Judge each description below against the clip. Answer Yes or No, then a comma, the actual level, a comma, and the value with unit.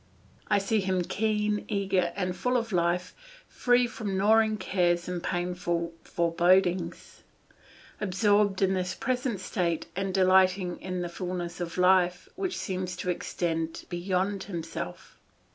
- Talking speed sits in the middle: No, slow, 130 wpm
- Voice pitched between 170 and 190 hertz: Yes, medium, 185 Hz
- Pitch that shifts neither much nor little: No, narrow, 2.3 semitones